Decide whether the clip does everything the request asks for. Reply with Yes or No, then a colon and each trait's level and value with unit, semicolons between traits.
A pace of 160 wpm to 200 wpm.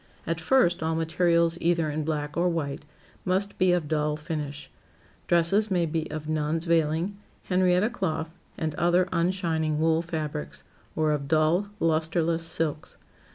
No: average, 145 wpm